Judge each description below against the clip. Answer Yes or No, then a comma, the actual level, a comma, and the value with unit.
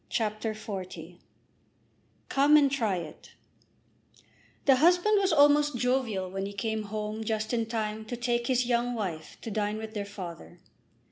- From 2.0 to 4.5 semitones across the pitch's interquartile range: Yes, average, 3.4 semitones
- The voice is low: No, high, 220 Hz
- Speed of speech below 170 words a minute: Yes, average, 150 wpm